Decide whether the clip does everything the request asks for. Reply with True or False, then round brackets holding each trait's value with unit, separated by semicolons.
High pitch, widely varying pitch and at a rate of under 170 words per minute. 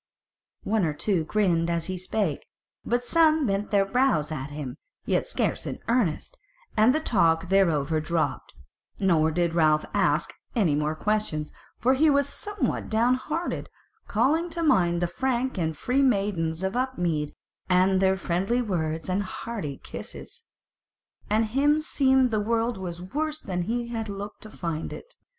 True (195 Hz; 6.9 semitones; 160 wpm)